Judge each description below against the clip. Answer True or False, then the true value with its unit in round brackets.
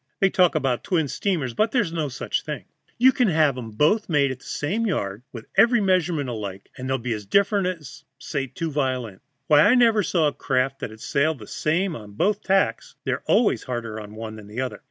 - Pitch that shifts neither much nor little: False (7.9 semitones)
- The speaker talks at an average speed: False (220 wpm)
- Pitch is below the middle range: False (145 Hz)